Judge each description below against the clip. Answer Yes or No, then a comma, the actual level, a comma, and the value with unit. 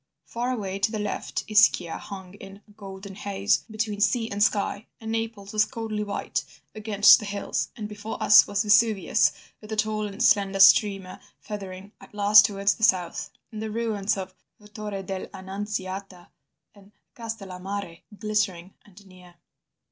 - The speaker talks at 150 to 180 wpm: Yes, average, 155 wpm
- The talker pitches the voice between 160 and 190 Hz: No, high, 205 Hz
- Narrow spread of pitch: Yes, narrow, 1.7 semitones